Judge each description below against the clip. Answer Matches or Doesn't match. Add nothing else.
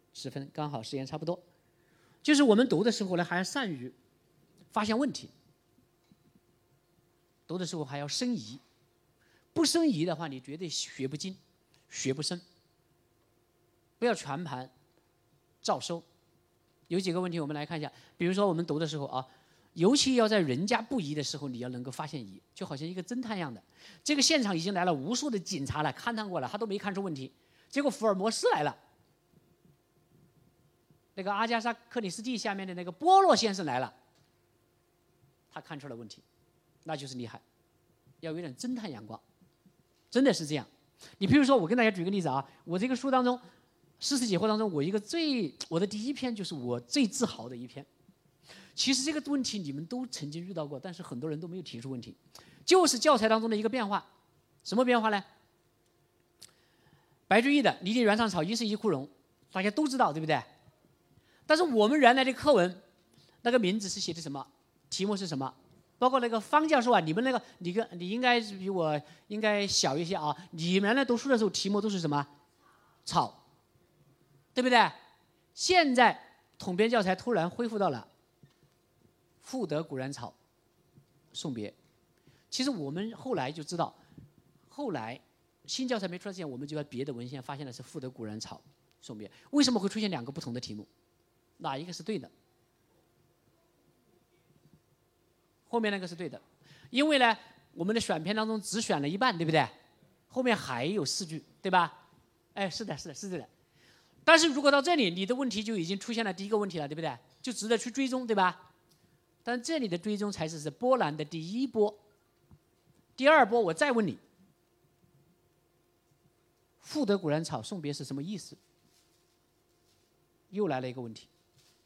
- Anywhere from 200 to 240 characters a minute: Doesn't match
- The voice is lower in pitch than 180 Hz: Doesn't match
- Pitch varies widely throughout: Matches